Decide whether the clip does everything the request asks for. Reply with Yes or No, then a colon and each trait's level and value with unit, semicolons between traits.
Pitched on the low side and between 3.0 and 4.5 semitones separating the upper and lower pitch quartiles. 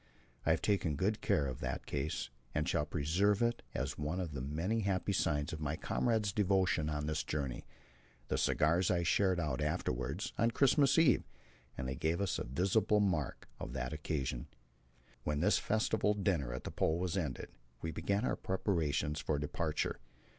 No: very low, 85 Hz; average, 5.2 semitones